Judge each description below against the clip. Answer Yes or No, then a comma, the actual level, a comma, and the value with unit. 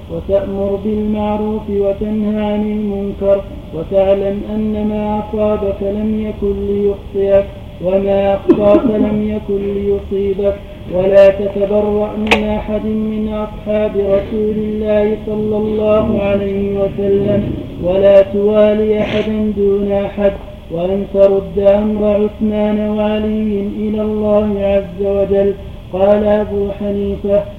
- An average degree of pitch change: No, narrow, 1.2 semitones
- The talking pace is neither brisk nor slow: Yes, average, 100 wpm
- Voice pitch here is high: Yes, high, 205 Hz